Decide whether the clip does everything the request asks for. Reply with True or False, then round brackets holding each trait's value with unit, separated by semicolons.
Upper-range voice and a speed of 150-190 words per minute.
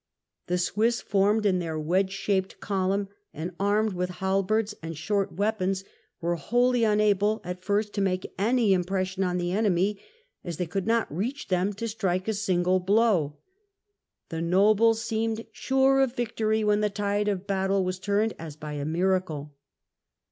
True (195 Hz; 160 wpm)